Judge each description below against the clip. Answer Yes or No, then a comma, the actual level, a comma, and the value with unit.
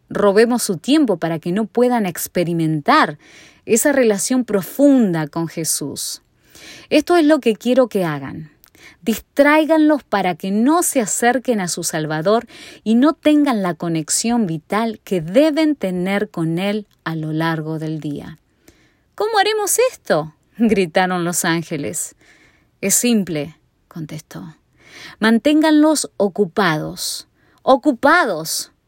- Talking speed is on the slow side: Yes, slow, 120 wpm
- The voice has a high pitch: Yes, high, 205 Hz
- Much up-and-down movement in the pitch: Yes, wide, 7.7 semitones